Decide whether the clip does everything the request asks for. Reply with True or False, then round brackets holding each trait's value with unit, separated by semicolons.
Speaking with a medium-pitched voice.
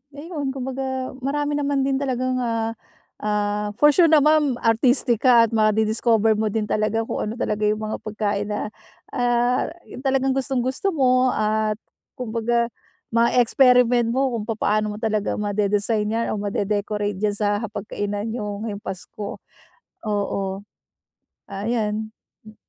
False (225 Hz)